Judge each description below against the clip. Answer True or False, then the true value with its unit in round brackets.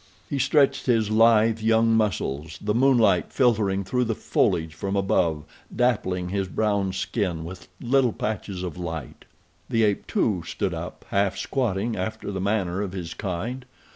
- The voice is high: False (100 Hz)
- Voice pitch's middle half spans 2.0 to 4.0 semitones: True (3.6 semitones)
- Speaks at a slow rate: False (155 wpm)